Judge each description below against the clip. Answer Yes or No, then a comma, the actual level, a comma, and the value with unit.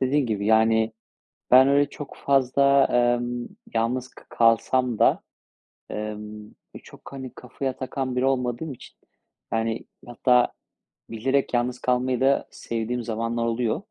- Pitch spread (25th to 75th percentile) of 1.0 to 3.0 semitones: Yes, narrow, 2.5 semitones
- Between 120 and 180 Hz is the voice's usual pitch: Yes, low, 125 Hz